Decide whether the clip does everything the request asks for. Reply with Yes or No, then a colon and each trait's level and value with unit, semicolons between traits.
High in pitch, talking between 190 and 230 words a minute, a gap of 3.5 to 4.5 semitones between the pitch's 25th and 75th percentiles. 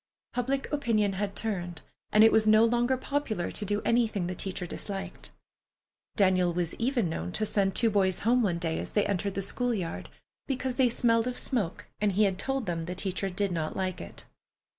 Yes: high, 205 Hz; average, 200 wpm; average, 4.2 semitones